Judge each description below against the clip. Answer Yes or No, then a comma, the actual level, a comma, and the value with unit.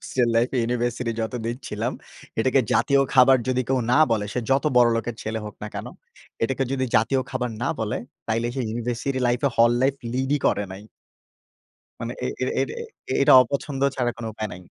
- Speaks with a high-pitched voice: No, low, 125 Hz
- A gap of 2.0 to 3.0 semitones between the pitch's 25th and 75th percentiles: Yes, narrow, 2.6 semitones